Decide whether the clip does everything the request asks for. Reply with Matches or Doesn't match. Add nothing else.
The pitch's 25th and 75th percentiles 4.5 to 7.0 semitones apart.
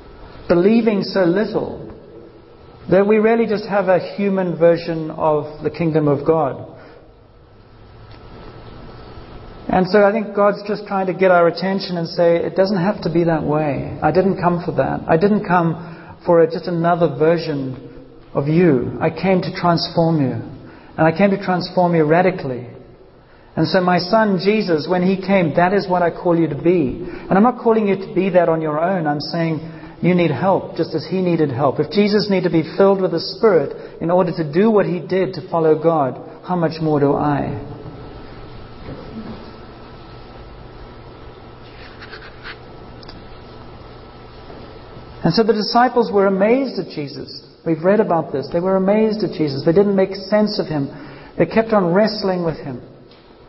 Doesn't match